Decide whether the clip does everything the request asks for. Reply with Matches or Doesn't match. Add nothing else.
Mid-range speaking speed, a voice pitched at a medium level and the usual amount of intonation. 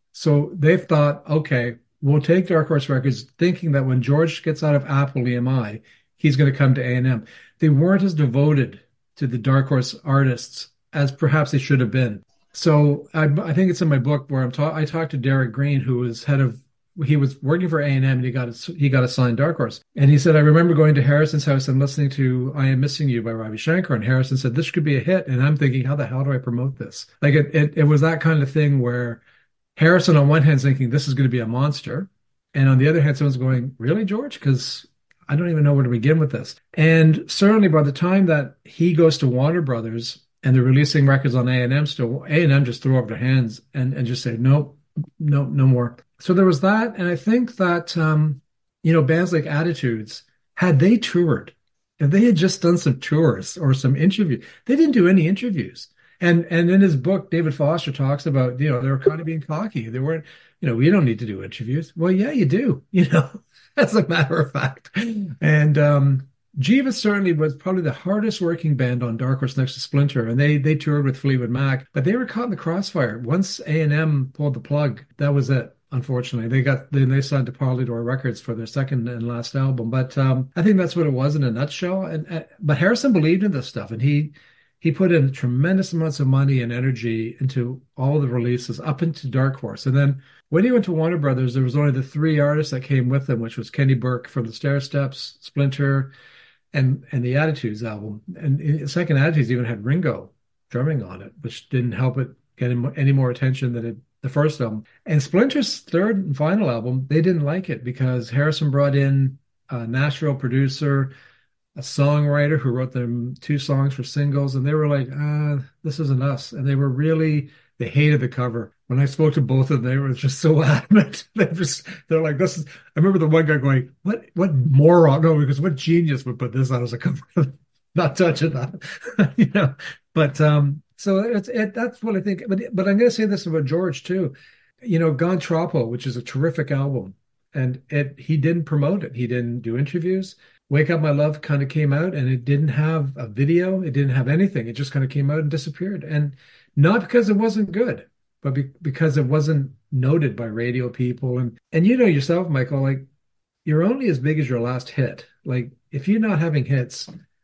Doesn't match